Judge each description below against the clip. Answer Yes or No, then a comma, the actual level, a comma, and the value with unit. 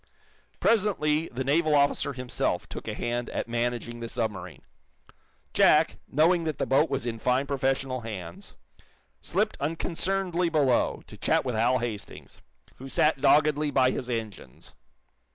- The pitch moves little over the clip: No, average, 4.3 semitones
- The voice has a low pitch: Yes, low, 130 Hz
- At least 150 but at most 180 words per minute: No, average, 140 wpm